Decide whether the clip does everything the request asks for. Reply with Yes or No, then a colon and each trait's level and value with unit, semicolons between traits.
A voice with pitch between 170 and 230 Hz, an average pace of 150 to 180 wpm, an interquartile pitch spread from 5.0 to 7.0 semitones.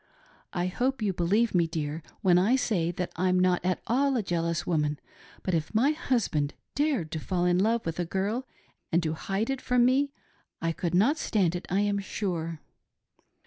No: medium, 185 Hz; average, 190 wpm; wide, 5.6 semitones